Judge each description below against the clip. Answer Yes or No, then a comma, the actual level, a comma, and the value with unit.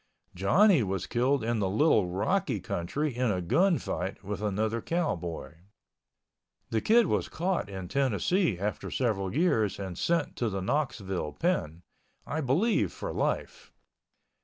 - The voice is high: No, low, 110 Hz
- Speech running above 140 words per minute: No, slow, 135 wpm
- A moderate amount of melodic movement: No, wide, 8.3 semitones